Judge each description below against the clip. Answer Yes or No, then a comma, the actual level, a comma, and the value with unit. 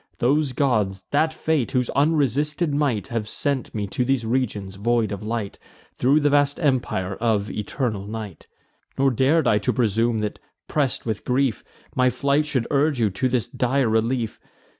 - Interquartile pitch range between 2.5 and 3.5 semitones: No, average, 4.3 semitones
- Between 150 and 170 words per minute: Yes, average, 165 wpm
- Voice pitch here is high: No, low, 125 Hz